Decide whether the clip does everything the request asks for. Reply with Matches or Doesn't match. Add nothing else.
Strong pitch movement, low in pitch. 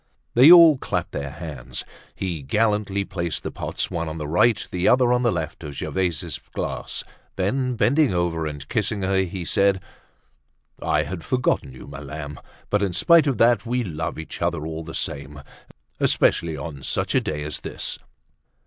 Matches